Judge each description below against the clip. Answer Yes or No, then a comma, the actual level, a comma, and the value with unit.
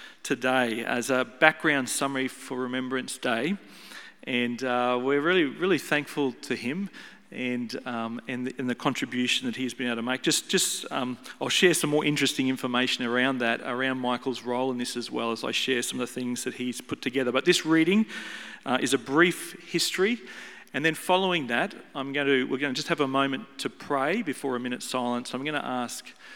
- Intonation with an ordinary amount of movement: Yes, average, 3.0 semitones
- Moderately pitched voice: No, low, 130 Hz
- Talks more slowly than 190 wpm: No, fast, 205 wpm